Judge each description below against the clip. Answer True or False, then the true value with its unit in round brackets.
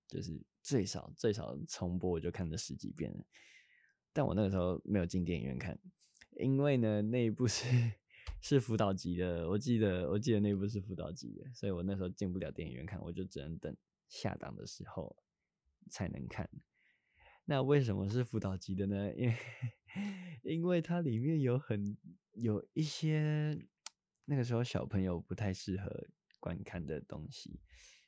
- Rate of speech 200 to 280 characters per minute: True (255 characters per minute)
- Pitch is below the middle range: True (105 Hz)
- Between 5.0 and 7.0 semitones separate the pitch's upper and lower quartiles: True (5.6 semitones)